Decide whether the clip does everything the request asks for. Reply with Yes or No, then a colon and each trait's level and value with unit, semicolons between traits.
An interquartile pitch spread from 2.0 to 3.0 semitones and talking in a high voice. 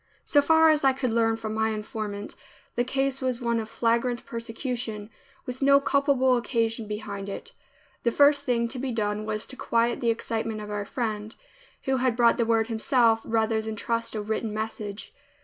Yes: narrow, 2.6 semitones; high, 230 Hz